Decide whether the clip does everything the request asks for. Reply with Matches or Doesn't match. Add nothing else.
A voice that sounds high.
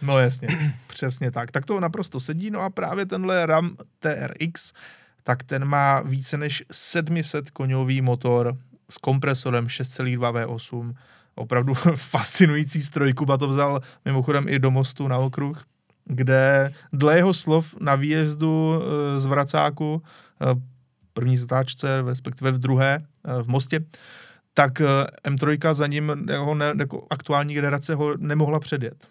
Doesn't match